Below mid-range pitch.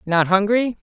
No: high, 205 Hz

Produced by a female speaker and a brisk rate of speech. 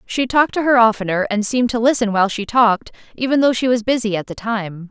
Yes: female; fast, 245 wpm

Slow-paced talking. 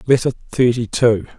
Yes: slow, 130 wpm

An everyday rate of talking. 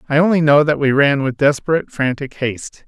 No: fast, 210 wpm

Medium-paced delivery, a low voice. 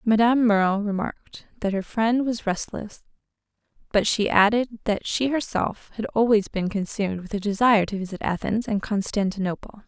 No: average, 160 wpm; high, 210 Hz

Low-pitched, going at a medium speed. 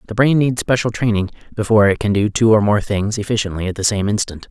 No: low, 105 Hz; fast, 240 wpm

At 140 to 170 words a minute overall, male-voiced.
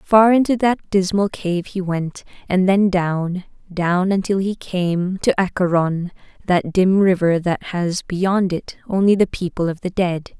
No: average, 165 wpm; female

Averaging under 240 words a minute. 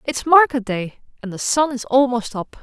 Yes: fast, 205 wpm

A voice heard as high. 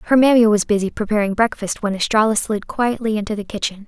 Yes: high, 215 Hz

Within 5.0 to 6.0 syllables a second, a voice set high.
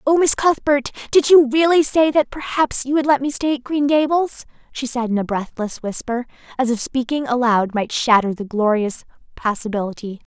Yes: 5.1 syllables/s; very high, 260 Hz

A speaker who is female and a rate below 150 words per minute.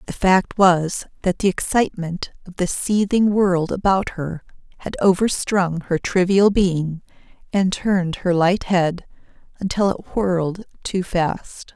Yes: female; average, 140 wpm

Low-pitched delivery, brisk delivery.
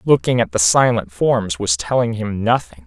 No: low, 105 Hz; average, 190 wpm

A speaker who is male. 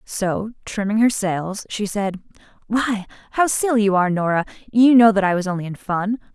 No: female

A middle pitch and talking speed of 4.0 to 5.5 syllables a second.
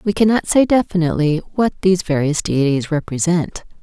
No: medium, 175 Hz; 5.7 syllables/s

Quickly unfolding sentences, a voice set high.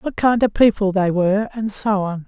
Yes: fast, 240 wpm; high, 205 Hz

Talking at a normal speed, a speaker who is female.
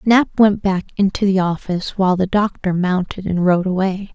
Yes: average, 190 wpm; female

